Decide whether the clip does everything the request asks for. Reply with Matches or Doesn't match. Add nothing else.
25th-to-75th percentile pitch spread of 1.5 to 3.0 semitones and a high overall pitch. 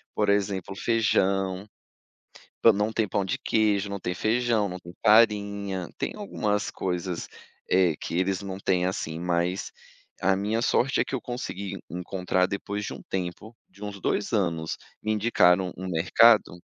Doesn't match